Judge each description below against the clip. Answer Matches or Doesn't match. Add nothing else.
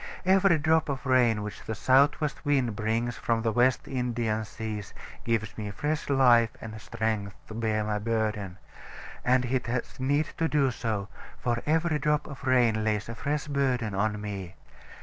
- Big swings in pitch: Doesn't match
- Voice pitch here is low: Matches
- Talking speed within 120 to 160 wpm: Doesn't match